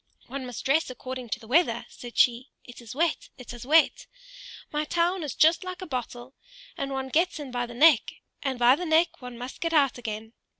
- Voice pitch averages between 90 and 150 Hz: No, very high, 260 Hz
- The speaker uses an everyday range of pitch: Yes, average, 4.5 semitones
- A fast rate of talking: Yes, fast, 215 wpm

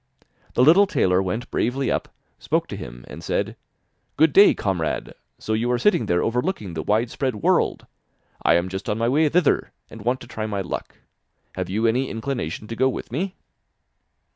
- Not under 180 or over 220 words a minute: Yes, average, 190 wpm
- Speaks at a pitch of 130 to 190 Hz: No, low, 115 Hz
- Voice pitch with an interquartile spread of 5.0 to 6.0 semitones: Yes, wide, 5.5 semitones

